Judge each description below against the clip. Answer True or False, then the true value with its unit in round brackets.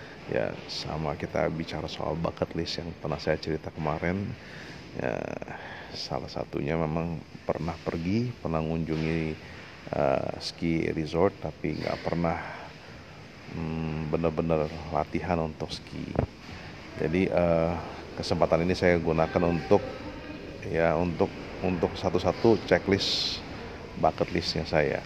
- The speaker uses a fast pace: False (115 wpm)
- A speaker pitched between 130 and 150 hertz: False (85 Hz)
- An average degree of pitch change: False (1.8 semitones)